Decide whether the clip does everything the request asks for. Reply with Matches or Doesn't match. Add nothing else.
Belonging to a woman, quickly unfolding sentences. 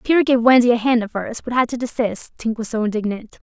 Matches